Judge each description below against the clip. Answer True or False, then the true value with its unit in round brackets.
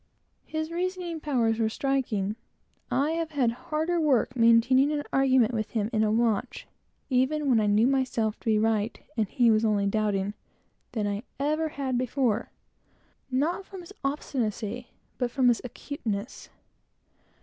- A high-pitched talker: True (245 Hz)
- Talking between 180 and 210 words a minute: False (150 wpm)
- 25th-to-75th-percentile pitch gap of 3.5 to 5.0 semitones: True (4.6 semitones)